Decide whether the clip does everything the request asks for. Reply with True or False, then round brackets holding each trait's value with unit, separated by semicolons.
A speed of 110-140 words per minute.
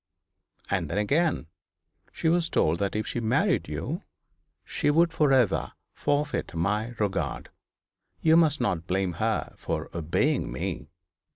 True (135 wpm)